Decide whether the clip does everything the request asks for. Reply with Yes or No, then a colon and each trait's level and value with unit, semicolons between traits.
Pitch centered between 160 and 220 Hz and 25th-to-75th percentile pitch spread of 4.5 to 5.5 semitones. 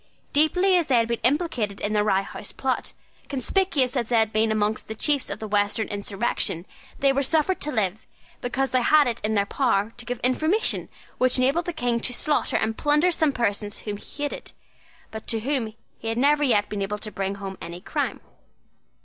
No: high, 235 Hz; average, 5.2 semitones